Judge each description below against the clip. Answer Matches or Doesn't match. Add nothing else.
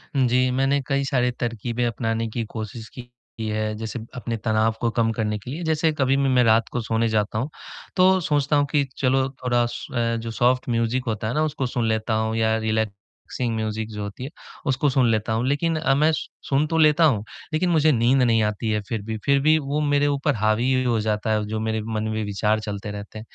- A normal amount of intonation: Matches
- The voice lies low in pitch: Matches